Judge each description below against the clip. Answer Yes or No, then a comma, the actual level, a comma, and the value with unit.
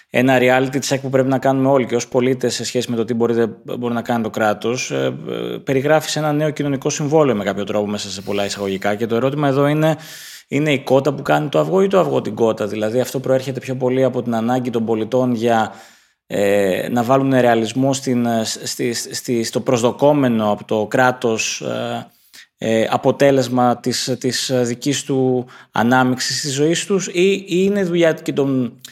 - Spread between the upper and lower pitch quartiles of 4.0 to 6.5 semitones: No, average, 3.1 semitones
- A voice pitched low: Yes, low, 125 Hz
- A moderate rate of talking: No, fast, 195 wpm